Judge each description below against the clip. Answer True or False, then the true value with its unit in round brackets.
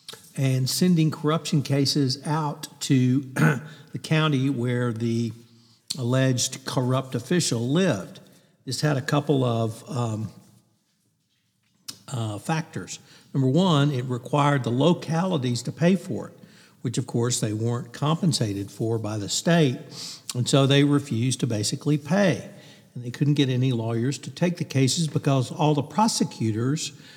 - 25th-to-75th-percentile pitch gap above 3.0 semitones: True (4.1 semitones)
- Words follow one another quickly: False (140 wpm)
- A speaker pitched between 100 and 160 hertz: True (140 Hz)